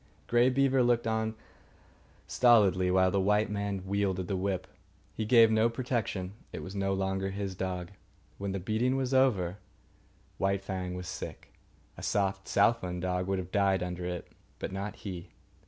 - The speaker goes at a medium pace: Yes, average, 165 wpm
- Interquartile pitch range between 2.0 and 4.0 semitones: Yes, average, 3.1 semitones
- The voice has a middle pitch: No, very low, 95 Hz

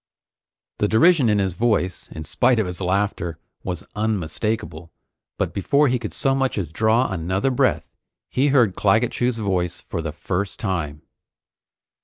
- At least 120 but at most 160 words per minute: Yes, average, 155 wpm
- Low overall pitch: Yes, low, 100 Hz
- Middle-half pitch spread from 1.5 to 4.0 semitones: No, average, 5.2 semitones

